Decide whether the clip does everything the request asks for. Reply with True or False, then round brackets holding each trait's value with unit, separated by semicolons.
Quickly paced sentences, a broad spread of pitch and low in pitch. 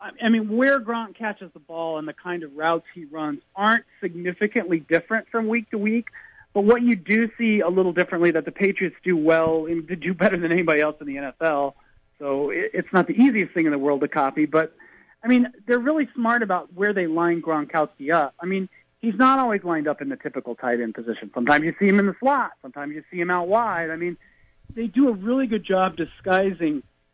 False (225 wpm; 6.0 semitones; 180 Hz)